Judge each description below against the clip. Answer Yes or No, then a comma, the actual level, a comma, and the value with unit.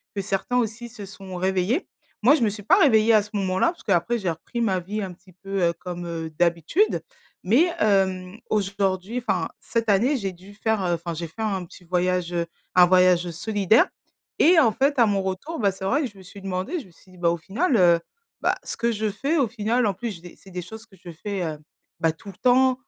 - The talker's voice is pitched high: Yes, high, 195 Hz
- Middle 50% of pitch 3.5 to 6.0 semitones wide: Yes, average, 4.1 semitones